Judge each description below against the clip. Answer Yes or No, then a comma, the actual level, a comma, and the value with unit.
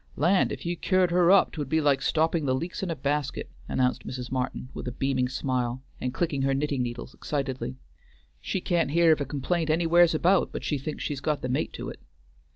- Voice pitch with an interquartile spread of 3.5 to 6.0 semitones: Yes, average, 4.5 semitones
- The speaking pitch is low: No, medium, 145 Hz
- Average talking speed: No, fast, 215 wpm